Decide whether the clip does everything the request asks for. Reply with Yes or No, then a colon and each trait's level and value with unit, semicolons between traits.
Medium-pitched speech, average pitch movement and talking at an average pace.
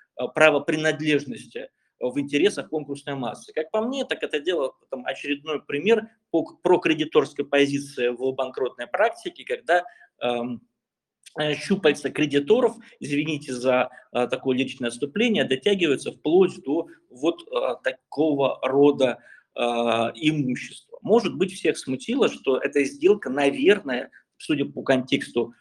No: medium, 145 Hz; wide, 9.0 semitones; average, 120 wpm